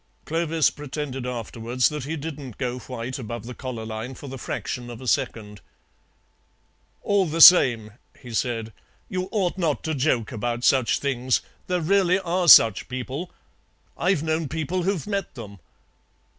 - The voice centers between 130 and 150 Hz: Yes, low, 135 Hz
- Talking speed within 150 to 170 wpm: Yes, average, 155 wpm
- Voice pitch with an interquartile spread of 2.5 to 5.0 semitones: No, wide, 5.4 semitones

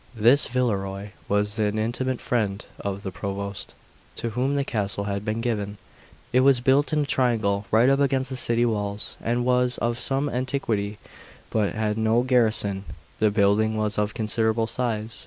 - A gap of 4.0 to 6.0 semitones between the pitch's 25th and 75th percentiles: No, average, 3.4 semitones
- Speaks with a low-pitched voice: Yes, low, 110 Hz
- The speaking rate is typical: Yes, average, 175 wpm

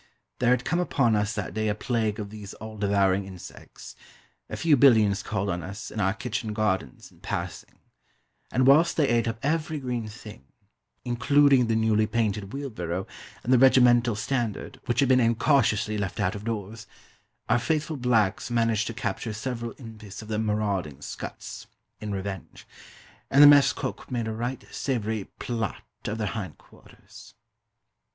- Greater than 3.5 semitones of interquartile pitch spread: No, average, 3.1 semitones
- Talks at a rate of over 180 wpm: No, average, 165 wpm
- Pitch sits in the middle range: No, low, 110 Hz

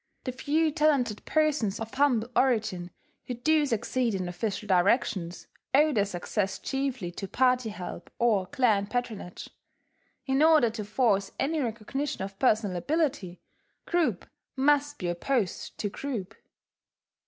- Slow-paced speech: Yes, slow, 130 wpm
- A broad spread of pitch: Yes, wide, 5.7 semitones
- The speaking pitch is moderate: No, high, 235 Hz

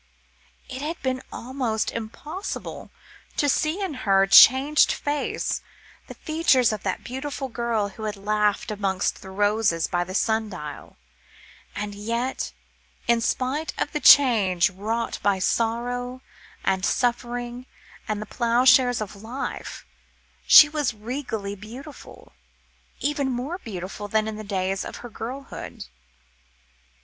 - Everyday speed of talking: No, slow, 130 wpm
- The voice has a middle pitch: No, high, 230 Hz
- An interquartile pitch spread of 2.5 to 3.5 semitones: No, average, 4.2 semitones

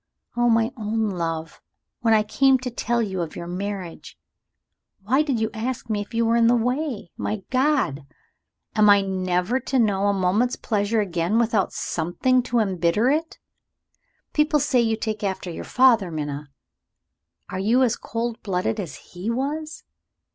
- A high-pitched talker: Yes, high, 220 Hz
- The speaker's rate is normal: Yes, average, 165 wpm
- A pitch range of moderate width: Yes, average, 4.4 semitones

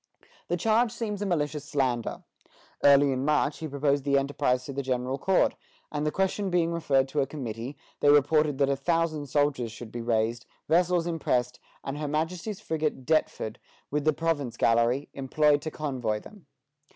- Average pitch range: Yes, average, 3.5 semitones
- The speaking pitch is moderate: Yes, medium, 145 Hz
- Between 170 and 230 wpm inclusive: Yes, average, 175 wpm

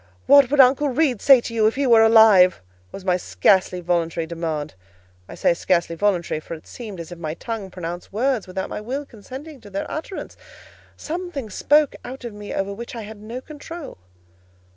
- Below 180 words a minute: No, average, 190 wpm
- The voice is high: Yes, high, 215 Hz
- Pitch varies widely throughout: Yes, wide, 6.5 semitones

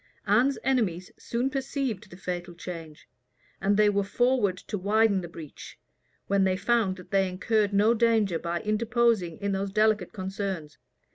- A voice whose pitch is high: Yes, high, 200 Hz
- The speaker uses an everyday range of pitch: Yes, average, 3.5 semitones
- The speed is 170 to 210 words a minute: No, average, 155 wpm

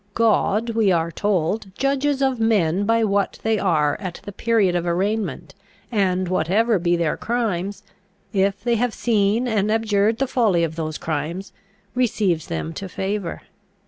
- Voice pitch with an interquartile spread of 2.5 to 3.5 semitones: No, average, 4.3 semitones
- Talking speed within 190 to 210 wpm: No, average, 155 wpm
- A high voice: Yes, high, 200 Hz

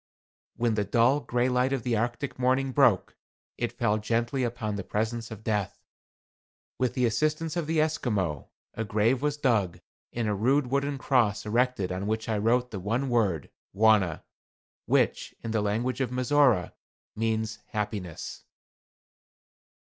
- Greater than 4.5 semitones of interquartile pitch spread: No, average, 3.3 semitones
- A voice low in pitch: Yes, low, 115 Hz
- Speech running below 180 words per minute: Yes, average, 150 wpm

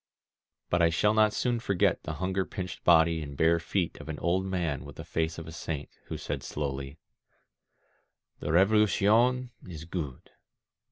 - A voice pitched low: Yes, very low, 85 Hz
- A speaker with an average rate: Yes, average, 165 wpm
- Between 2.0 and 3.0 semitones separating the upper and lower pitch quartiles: No, average, 3.6 semitones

